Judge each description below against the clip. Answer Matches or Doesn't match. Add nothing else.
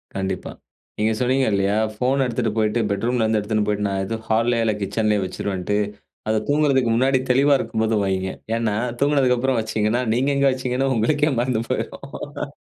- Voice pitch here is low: Matches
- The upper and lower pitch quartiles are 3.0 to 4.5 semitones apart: Matches